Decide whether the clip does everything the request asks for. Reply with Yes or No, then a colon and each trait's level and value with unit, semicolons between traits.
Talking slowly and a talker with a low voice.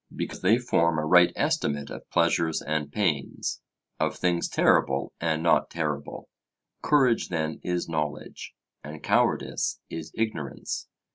Yes: slow, 130 wpm; very low, 80 Hz